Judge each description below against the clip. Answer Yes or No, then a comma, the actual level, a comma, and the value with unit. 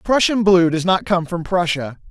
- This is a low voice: No, medium, 180 Hz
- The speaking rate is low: No, average, 200 wpm